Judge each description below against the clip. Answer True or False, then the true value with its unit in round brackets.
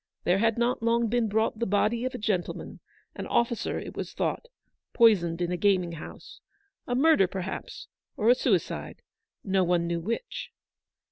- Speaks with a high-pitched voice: True (215 Hz)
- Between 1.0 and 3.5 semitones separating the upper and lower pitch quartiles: False (4.7 semitones)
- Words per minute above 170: False (165 wpm)